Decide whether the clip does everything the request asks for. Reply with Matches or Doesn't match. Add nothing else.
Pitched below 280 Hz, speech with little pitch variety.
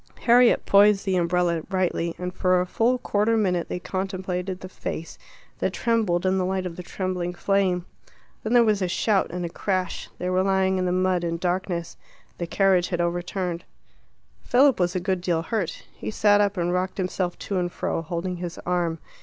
Matches